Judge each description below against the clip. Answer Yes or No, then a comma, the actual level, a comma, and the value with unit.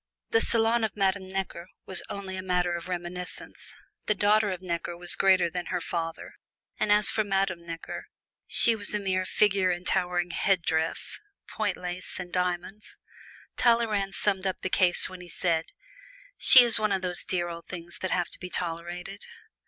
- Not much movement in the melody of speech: Yes, narrow, 2.3 semitones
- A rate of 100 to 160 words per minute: No, average, 175 wpm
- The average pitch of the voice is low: No, medium, 185 Hz